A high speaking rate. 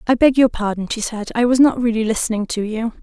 Yes: fast, 260 wpm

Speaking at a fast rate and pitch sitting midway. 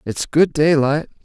No: average, 145 wpm; medium, 150 Hz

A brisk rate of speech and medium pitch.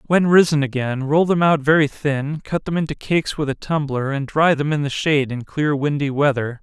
Yes: fast, 225 wpm; medium, 145 Hz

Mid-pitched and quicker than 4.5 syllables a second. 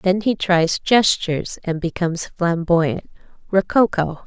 No: medium, 180 Hz; 4.0 syllables/s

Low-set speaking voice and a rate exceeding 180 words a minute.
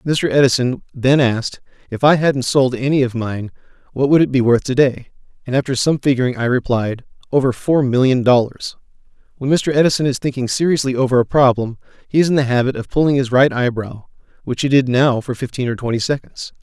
Yes: low, 130 Hz; average, 200 wpm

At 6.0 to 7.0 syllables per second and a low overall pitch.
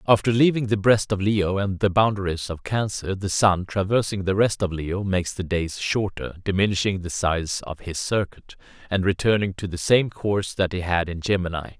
No: 5.1 syllables/s; very low, 95 Hz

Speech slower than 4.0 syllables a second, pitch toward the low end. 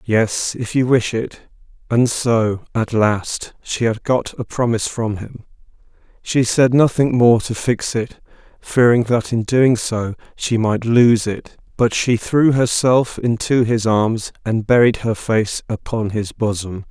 Yes: 3.8 syllables/s; low, 115 Hz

